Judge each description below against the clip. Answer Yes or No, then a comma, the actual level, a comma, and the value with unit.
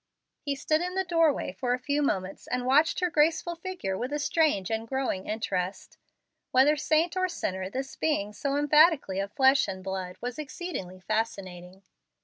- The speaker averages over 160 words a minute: Yes, average, 175 wpm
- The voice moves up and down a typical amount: No, wide, 8.0 semitones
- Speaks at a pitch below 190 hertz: No, very high, 265 Hz